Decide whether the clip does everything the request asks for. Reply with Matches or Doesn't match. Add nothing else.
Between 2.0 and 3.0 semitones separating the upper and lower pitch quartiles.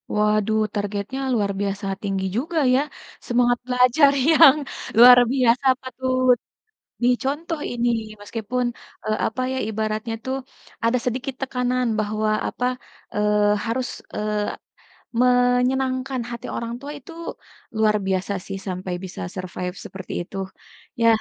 Doesn't match